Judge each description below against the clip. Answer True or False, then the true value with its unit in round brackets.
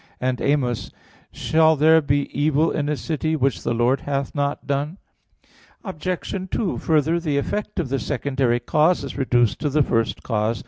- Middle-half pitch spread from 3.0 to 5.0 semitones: True (3.3 semitones)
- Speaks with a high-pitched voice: False (145 Hz)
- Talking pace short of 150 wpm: False (175 wpm)